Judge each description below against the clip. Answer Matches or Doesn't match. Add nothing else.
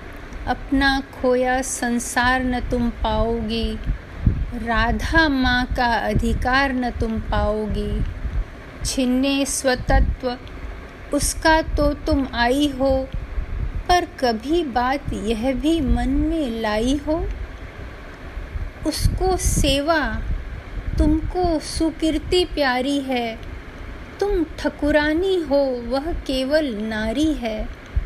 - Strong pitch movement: Doesn't match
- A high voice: Matches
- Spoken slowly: Matches